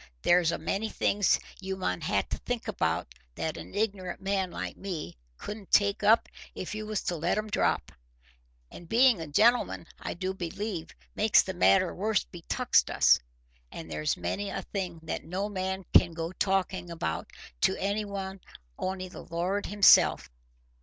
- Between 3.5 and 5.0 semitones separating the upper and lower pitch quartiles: No, average, 3.1 semitones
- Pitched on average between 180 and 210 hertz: Yes, high, 190 Hz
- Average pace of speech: Yes, average, 165 wpm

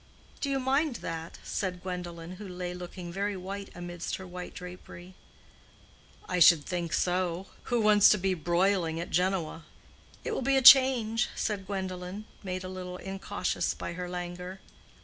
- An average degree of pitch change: No, narrow, 2.2 semitones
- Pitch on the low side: No, medium, 185 Hz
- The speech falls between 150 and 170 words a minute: Yes, average, 160 wpm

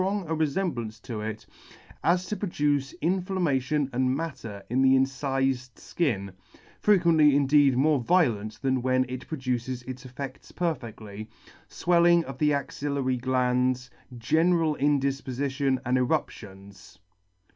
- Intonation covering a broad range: No, average, 3.8 semitones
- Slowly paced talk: Yes, slow, 120 wpm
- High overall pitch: No, low, 135 Hz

